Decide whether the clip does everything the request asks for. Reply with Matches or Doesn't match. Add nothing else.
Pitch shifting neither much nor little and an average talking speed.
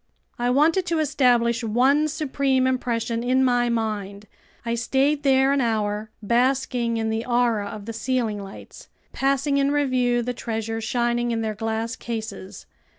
Matches